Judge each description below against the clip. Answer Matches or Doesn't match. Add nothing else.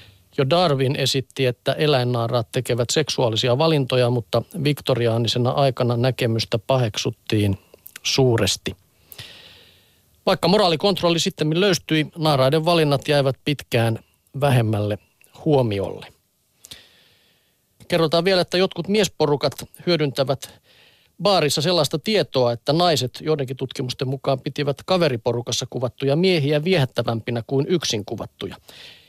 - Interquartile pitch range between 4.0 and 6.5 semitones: Matches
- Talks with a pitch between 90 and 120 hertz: Doesn't match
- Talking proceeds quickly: Doesn't match